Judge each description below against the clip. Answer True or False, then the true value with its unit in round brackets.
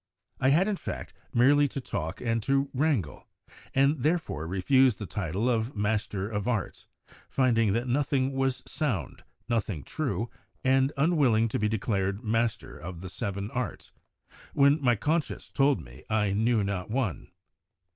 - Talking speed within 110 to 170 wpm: True (150 wpm)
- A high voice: False (115 Hz)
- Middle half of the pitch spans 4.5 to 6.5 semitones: True (5.1 semitones)